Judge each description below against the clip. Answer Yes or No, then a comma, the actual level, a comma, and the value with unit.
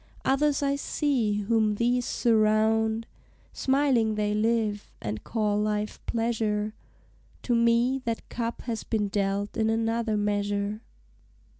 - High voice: Yes, high, 220 Hz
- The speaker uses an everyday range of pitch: No, narrow, 2.0 semitones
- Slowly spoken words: Yes, slow, 120 wpm